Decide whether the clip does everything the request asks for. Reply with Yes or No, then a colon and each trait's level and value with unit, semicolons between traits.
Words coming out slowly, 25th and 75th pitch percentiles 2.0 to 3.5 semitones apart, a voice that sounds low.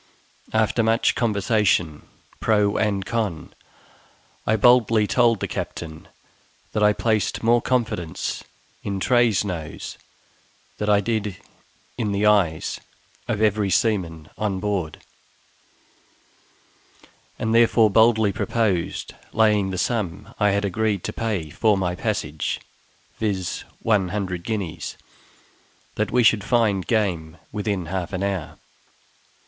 Yes: slow, 120 wpm; average, 2.9 semitones; low, 105 Hz